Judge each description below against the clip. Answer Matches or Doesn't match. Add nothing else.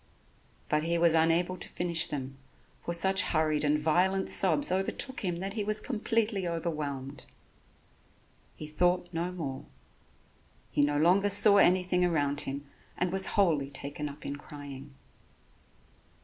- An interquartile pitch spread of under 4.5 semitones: Matches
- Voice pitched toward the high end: Doesn't match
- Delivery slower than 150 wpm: Matches